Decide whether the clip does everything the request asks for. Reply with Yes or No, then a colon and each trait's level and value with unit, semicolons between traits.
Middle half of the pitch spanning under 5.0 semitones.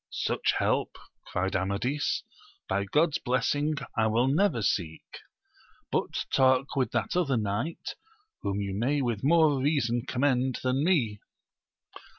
No: average, 5.3 semitones